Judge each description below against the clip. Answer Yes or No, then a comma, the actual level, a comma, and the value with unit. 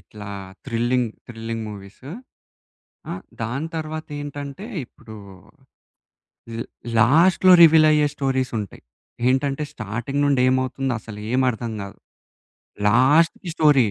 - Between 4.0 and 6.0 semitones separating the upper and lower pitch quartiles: Yes, average, 4.4 semitones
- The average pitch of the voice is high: No, low, 130 Hz